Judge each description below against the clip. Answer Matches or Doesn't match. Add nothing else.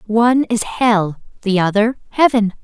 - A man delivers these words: Doesn't match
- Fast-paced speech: Doesn't match